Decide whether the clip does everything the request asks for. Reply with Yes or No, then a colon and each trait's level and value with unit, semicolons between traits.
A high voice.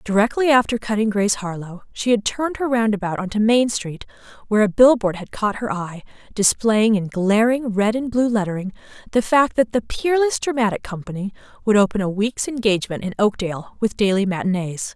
Yes: high, 215 Hz